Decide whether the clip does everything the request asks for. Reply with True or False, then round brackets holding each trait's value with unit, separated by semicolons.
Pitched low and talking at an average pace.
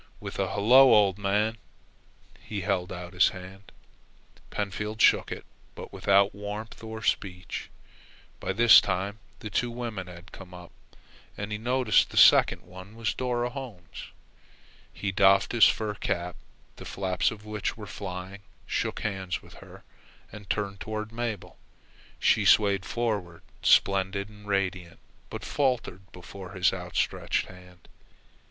True (100 Hz; 145 wpm)